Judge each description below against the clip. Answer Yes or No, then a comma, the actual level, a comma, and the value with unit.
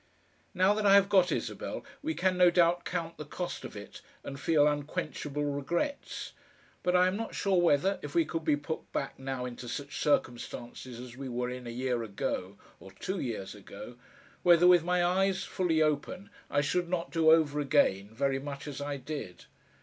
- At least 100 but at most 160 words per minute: No, average, 190 wpm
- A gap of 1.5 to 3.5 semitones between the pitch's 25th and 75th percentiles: No, average, 5.3 semitones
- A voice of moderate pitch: Yes, medium, 150 Hz